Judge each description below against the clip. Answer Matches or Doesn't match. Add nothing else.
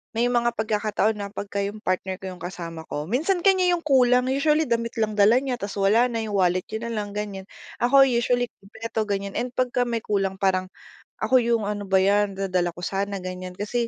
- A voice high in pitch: Matches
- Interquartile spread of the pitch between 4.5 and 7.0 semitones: Doesn't match